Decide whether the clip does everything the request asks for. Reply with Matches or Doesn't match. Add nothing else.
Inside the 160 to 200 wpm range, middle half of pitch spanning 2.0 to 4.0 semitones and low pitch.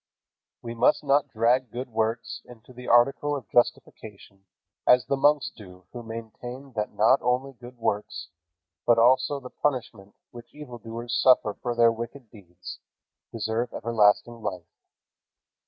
Doesn't match